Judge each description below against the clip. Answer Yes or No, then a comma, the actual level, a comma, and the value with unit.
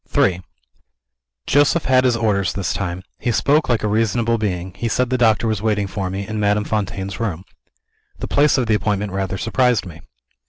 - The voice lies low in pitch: Yes, low, 105 Hz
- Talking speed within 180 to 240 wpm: Yes, average, 190 wpm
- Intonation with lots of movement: No, average, 3.3 semitones